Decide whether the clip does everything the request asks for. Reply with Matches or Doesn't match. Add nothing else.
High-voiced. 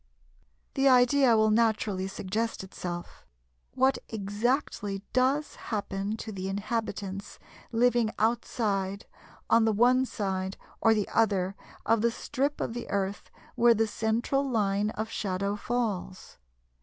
Matches